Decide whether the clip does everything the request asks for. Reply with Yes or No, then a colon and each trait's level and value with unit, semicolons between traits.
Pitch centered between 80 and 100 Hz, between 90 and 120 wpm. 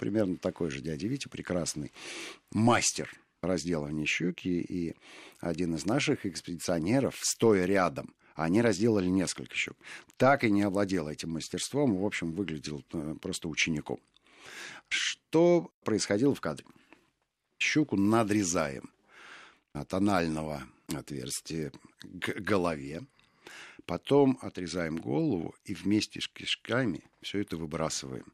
Yes: very low, 90 Hz; slow, 110 wpm